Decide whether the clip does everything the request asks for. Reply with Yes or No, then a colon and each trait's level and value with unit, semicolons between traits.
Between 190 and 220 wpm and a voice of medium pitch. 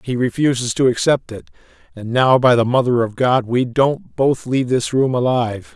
No: average, 200 wpm; low, 125 Hz